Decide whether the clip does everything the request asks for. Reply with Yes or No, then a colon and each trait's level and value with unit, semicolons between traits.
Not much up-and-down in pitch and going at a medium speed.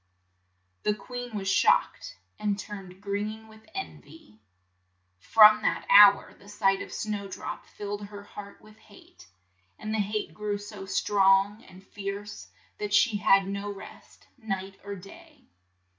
Yes: narrow, 1.4 semitones; average, 145 wpm